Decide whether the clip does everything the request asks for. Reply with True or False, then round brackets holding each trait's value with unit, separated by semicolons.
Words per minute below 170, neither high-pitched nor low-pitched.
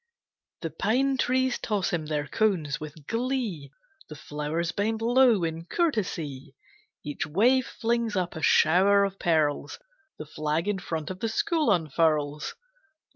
True (140 wpm; 180 Hz)